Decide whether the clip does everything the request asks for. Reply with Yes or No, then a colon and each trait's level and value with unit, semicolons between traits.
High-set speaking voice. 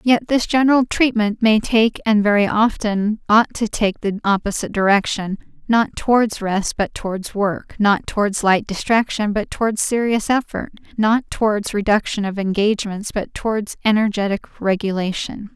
Yes: high, 210 Hz